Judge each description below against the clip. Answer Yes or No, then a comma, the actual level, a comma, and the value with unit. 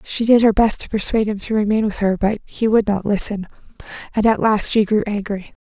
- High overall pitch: Yes, high, 210 Hz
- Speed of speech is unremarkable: No, fast, 235 wpm